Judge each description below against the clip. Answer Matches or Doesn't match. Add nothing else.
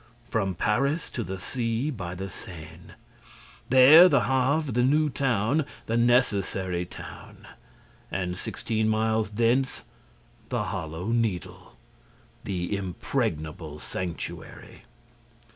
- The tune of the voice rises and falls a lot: Matches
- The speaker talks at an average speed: Doesn't match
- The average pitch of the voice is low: Matches